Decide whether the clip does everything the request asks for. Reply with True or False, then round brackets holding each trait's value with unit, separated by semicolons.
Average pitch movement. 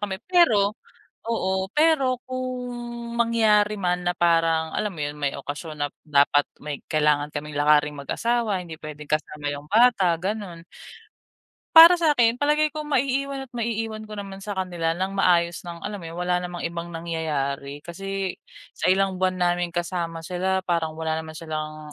False (5.7 semitones)